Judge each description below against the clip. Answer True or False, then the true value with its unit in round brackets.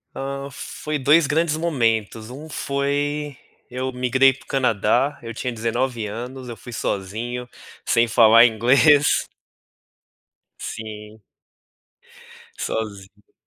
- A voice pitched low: True (125 Hz)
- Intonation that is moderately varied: True (3.8 semitones)